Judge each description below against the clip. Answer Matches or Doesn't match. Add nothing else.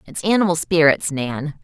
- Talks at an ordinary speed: Matches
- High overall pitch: Doesn't match